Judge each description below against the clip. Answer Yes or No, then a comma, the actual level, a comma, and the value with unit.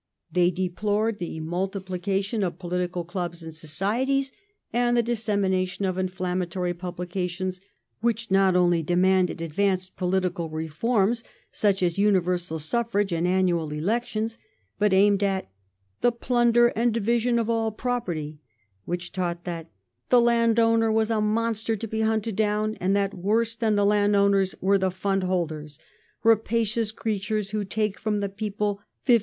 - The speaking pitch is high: Yes, high, 195 Hz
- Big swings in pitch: No, average, 3.6 semitones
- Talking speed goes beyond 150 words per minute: No, average, 145 wpm